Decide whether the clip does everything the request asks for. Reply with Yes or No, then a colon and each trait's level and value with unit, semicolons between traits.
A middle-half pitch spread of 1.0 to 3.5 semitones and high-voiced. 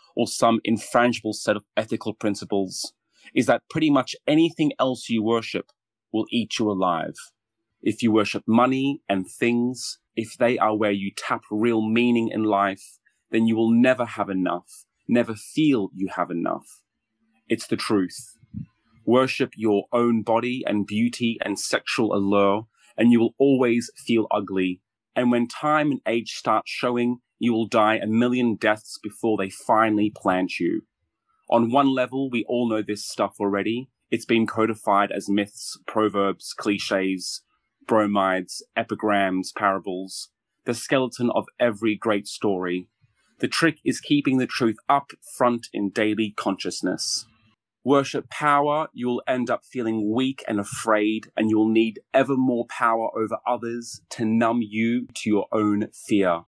No: narrow, 2.4 semitones; low, 115 Hz